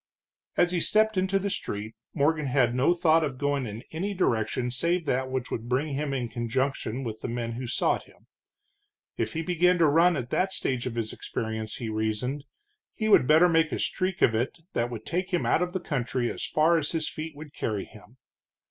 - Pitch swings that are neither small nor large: No, wide, 5.8 semitones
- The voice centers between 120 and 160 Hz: Yes, medium, 140 Hz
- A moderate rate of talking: No, fast, 210 wpm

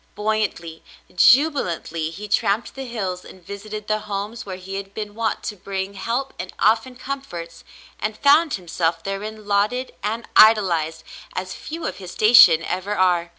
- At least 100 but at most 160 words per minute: Yes, average, 155 wpm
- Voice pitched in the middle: No, high, 200 Hz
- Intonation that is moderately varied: Yes, average, 3.3 semitones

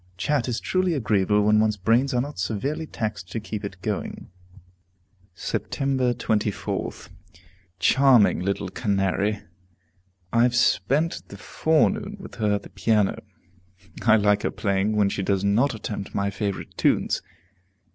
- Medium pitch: No, low, 105 Hz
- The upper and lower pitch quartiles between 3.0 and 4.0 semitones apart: Yes, average, 3.5 semitones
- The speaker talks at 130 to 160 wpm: Yes, average, 140 wpm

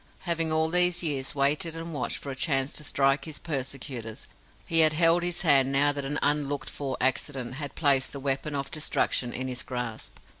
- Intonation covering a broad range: No, average, 2.9 semitones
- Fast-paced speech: No, average, 195 wpm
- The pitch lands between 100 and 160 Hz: Yes, medium, 140 Hz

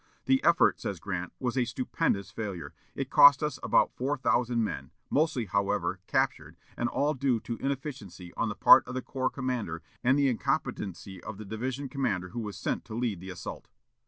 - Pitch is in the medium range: No, low, 120 Hz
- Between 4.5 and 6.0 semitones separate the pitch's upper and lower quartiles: Yes, average, 5.3 semitones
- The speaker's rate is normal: Yes, average, 190 wpm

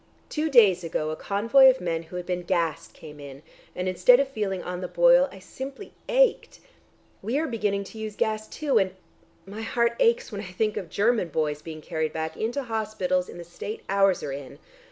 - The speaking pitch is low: No, high, 200 Hz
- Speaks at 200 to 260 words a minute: Yes, fast, 205 wpm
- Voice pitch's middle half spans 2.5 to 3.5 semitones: No, wide, 5.4 semitones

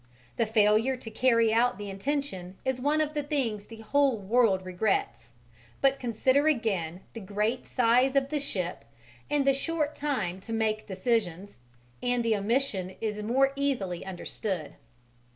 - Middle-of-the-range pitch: No, high, 230 Hz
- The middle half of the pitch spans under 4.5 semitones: No, average, 5.3 semitones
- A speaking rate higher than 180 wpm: No, average, 150 wpm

